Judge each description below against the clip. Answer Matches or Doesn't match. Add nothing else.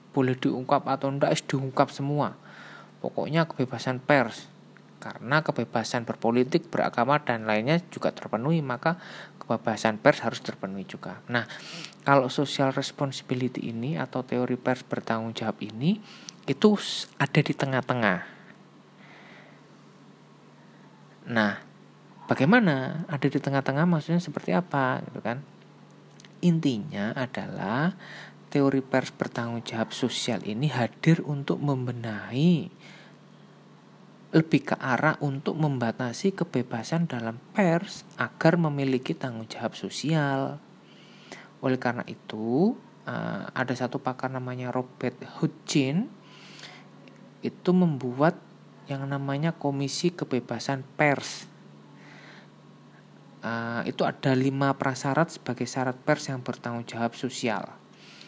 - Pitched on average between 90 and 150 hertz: Matches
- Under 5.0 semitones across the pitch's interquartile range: Matches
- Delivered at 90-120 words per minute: Matches